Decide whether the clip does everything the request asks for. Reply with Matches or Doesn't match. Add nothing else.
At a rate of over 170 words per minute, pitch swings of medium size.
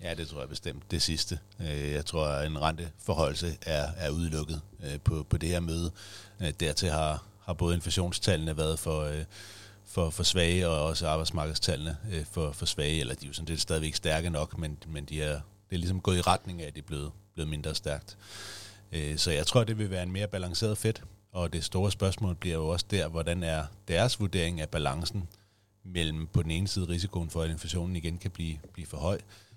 Matches